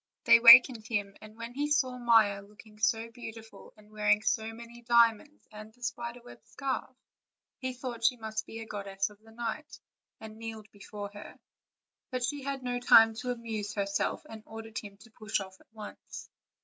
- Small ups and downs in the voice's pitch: Yes, narrow, 2.1 semitones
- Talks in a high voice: Yes, high, 225 Hz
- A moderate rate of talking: Yes, average, 180 wpm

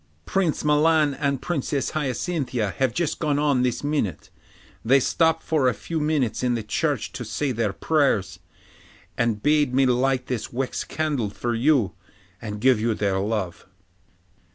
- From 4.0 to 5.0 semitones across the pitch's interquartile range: Yes, average, 4.7 semitones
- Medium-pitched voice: No, low, 130 Hz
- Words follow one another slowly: No, average, 155 wpm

